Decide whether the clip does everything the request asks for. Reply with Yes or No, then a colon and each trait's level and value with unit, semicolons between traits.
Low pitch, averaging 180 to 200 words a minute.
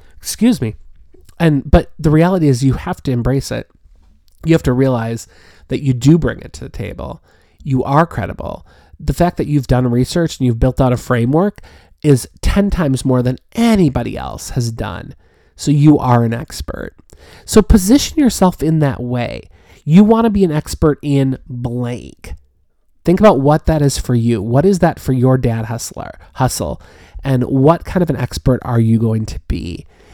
Yes: low, 130 Hz; average, 185 wpm